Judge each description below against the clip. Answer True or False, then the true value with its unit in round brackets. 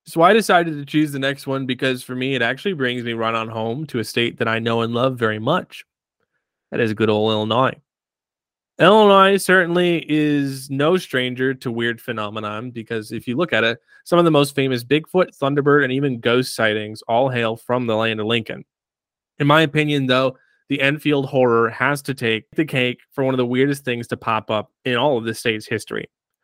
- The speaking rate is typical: False (210 wpm)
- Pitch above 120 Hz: True (130 Hz)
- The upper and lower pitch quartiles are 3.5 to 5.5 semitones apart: True (3.9 semitones)